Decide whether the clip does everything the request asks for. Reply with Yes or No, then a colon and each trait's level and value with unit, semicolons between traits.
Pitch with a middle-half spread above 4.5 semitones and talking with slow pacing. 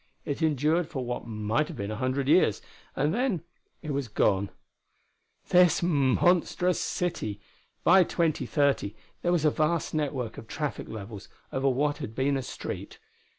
No: average, 5.2 semitones; average, 150 wpm